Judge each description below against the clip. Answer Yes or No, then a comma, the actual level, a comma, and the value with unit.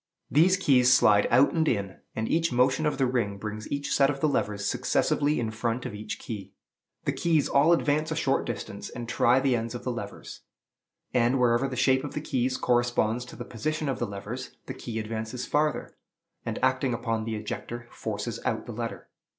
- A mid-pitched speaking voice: No, low, 125 Hz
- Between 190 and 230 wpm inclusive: Yes, average, 200 wpm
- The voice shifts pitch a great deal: No, average, 3.7 semitones